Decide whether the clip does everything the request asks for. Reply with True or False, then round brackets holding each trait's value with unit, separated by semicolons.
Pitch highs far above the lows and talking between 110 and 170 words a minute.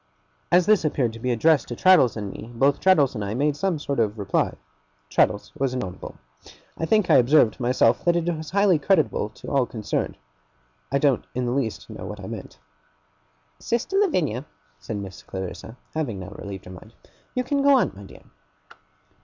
False (6.8 semitones; 185 wpm)